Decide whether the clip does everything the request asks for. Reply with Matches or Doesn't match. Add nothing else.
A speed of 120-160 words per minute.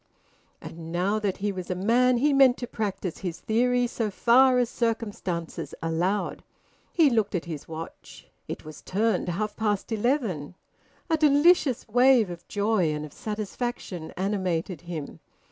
Matches